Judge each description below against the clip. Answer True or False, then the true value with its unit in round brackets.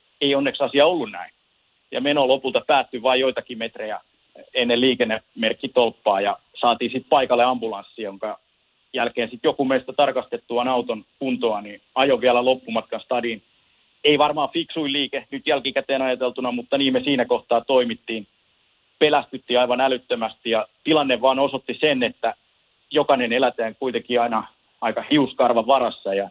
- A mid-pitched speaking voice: False (125 Hz)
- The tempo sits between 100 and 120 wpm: False (140 wpm)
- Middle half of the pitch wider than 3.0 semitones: False (2.4 semitones)